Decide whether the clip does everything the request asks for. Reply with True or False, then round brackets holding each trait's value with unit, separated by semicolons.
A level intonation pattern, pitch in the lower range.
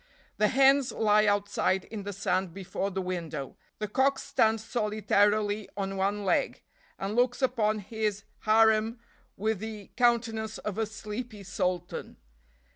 False (2.1 semitones; 210 Hz)